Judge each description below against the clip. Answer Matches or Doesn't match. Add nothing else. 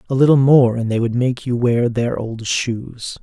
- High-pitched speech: Doesn't match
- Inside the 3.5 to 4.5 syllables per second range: Matches